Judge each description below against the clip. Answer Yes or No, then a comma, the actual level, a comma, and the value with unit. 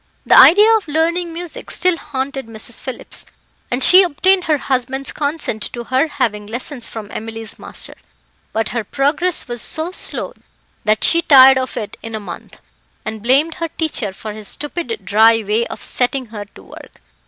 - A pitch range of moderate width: No, wide, 6.4 semitones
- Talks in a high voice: Yes, very high, 265 Hz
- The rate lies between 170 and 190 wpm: Yes, average, 175 wpm